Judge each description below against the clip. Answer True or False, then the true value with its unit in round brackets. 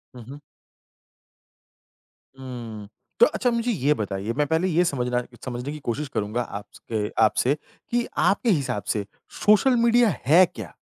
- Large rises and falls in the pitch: True (8.5 semitones)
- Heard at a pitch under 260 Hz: True (135 Hz)